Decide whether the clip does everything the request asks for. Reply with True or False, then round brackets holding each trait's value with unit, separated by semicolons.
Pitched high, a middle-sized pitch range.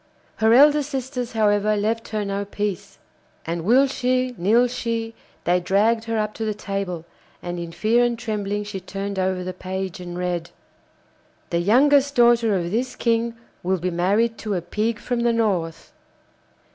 True (210 Hz; 4.0 semitones)